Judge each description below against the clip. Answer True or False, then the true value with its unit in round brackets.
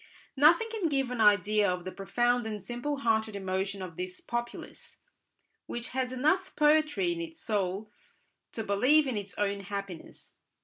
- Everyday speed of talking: True (160 wpm)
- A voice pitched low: False (225 Hz)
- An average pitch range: False (6.4 semitones)